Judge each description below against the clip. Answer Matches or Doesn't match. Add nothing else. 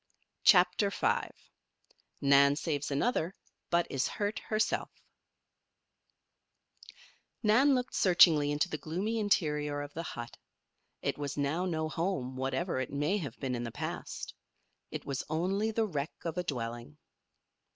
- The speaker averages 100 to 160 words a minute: Matches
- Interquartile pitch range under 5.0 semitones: Doesn't match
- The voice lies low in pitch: Doesn't match